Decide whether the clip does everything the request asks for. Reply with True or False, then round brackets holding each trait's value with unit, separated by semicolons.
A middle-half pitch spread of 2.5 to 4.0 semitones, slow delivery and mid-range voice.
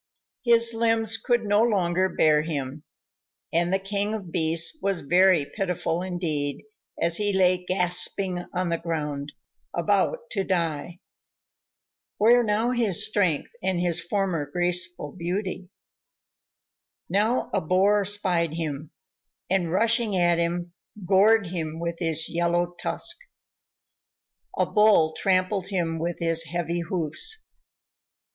True (3.3 semitones; 125 wpm; 180 Hz)